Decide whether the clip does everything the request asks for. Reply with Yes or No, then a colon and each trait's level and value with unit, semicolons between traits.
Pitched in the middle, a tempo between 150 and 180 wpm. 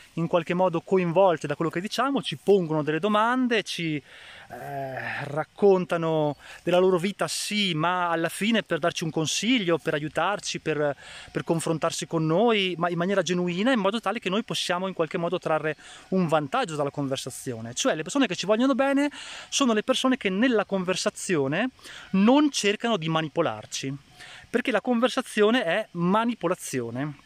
Yes: medium, 175 Hz; average, 160 wpm